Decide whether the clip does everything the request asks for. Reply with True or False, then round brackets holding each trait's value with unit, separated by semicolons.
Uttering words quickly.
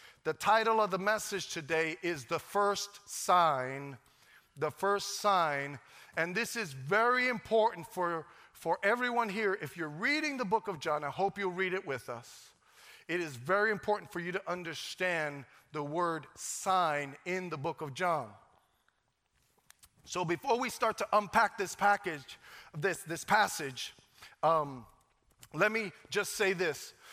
False (155 wpm)